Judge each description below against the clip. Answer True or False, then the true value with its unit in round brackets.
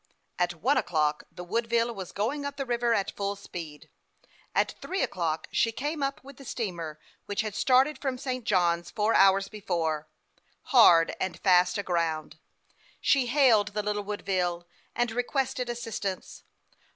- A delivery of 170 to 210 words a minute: False (150 wpm)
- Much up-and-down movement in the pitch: True (5.7 semitones)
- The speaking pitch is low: False (210 Hz)